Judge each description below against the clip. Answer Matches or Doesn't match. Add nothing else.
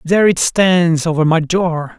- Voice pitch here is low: Doesn't match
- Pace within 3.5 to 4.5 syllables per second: Matches